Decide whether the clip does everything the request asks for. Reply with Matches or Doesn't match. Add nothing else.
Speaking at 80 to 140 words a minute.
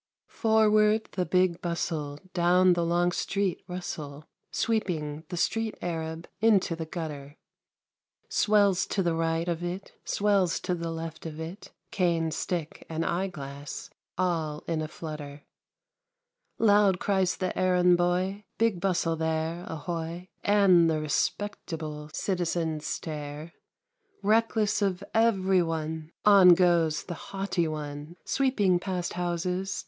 Matches